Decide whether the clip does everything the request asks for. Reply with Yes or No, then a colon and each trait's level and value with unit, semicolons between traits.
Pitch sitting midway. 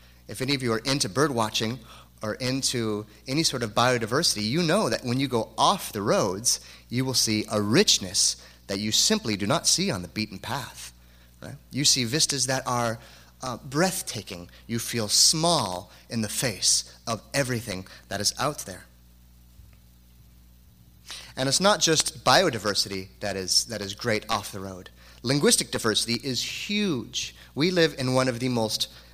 No: low, 110 Hz